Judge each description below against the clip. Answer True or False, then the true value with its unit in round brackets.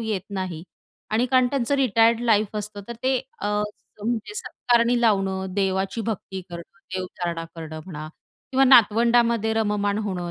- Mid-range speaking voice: False (210 Hz)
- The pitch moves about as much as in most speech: True (3.8 semitones)